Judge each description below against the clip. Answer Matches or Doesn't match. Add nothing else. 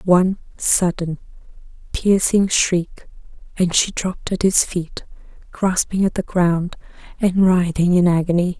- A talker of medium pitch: Matches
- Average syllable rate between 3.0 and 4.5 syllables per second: Matches